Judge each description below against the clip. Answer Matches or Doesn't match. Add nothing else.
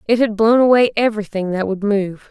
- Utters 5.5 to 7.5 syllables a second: Matches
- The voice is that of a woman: Matches